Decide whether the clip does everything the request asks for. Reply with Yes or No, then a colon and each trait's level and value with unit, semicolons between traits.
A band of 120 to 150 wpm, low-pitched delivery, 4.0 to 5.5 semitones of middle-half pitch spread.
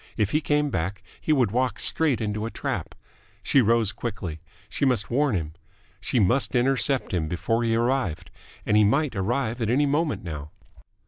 No: average, 180 wpm; low, 115 Hz; average, 5.1 semitones